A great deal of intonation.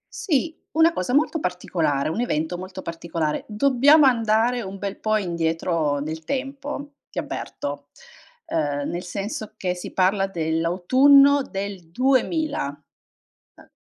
Yes: wide, 8.3 semitones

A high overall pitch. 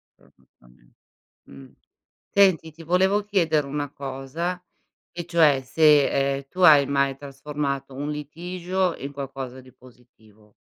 No: medium, 145 Hz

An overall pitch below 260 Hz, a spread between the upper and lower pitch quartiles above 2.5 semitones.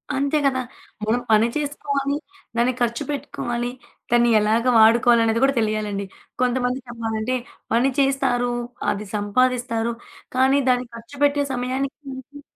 Yes: high, 245 Hz; average, 2.9 semitones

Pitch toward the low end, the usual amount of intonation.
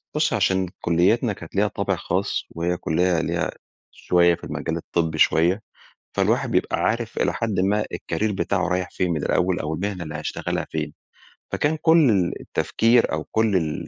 Yes: very low, 90 Hz; average, 3.7 semitones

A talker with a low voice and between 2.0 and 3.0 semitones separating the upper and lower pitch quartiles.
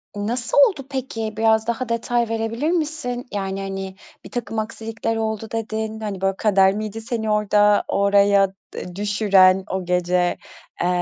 No: high, 215 Hz; narrow, 2.5 semitones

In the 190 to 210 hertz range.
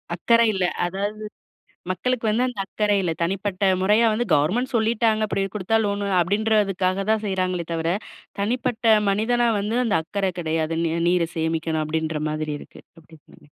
Yes: high, 195 Hz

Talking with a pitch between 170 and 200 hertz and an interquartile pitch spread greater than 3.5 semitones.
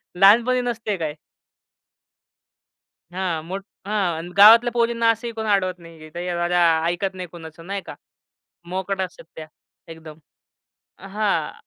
Yes: high, 190 Hz; average, 3.9 semitones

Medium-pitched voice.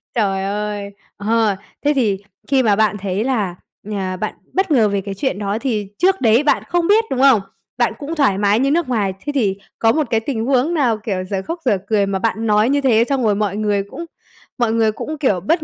No: high, 220 Hz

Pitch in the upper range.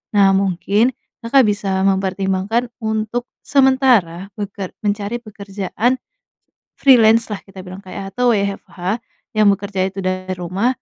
Yes: high, 200 Hz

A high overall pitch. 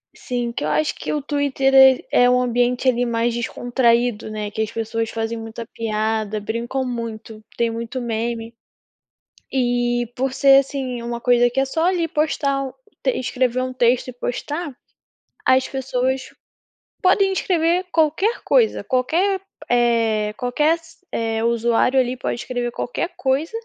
Yes: high, 245 Hz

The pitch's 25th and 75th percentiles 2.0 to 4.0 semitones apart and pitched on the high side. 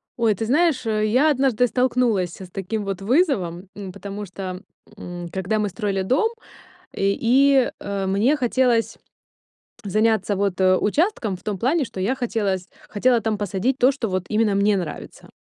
No: average, 4.5 semitones; high, 210 Hz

